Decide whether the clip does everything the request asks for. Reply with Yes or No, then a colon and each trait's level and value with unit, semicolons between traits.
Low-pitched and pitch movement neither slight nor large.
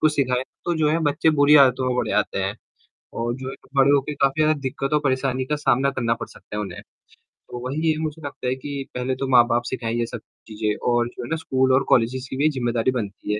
Yes: low, 130 Hz; average, 3.0 semitones